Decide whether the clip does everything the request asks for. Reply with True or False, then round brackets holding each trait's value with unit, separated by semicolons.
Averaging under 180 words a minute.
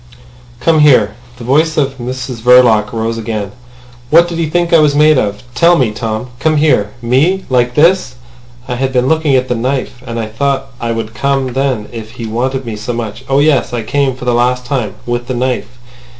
False (205 wpm)